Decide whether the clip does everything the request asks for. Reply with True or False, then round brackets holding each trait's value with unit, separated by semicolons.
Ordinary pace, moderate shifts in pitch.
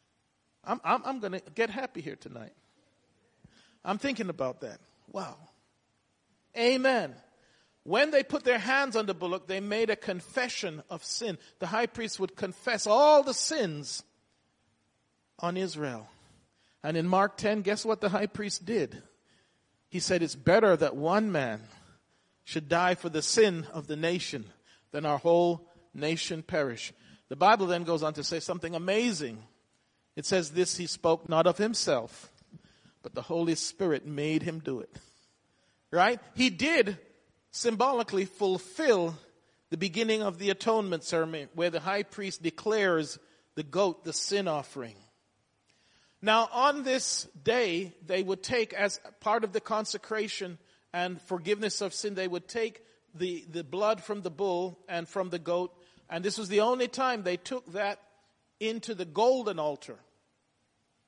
True (155 wpm; 4.6 semitones)